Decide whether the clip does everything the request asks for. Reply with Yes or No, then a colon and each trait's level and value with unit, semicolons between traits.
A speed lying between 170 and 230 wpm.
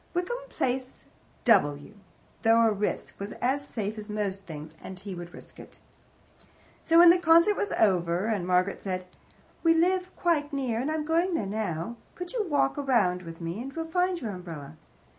Yes: average, 180 wpm